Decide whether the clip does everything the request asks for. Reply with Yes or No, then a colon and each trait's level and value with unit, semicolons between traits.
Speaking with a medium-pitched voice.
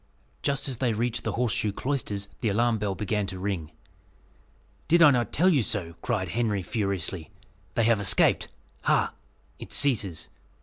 No: low, 110 Hz